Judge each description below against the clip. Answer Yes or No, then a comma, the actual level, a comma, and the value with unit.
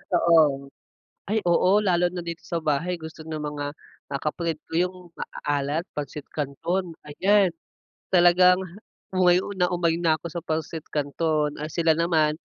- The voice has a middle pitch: Yes, medium, 165 Hz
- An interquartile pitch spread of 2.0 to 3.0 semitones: Yes, average, 2.7 semitones